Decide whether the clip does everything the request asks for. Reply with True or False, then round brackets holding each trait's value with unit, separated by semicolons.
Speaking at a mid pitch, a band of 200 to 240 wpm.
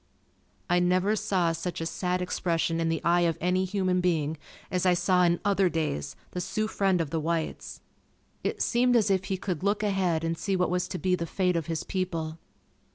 True (180 Hz; 205 wpm)